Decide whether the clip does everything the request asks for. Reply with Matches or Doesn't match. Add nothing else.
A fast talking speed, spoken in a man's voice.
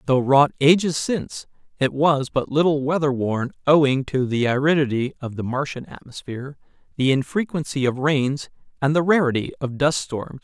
Doesn't match